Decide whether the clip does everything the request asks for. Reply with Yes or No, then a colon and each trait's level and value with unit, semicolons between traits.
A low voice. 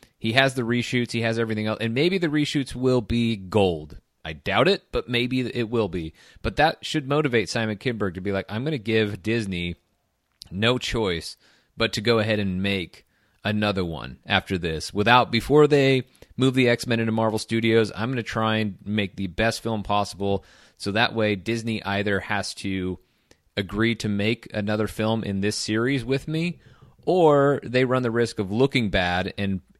Yes: low, 110 Hz